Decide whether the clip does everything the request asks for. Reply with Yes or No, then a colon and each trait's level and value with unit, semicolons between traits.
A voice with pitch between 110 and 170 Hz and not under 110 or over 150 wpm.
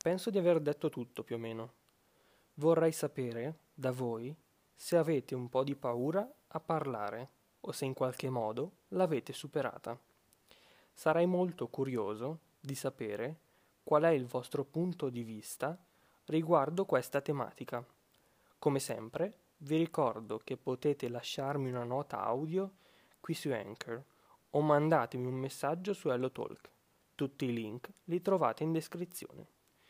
Yes: medium, 140 Hz; average, 135 wpm